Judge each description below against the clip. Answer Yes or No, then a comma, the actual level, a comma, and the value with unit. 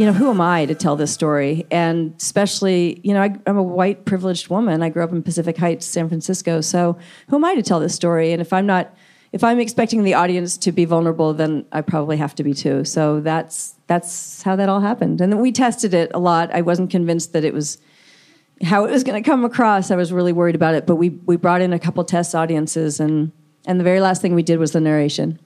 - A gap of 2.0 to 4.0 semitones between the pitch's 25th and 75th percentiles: Yes, average, 2.8 semitones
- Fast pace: Yes, fast, 250 wpm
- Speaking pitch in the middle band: Yes, medium, 175 Hz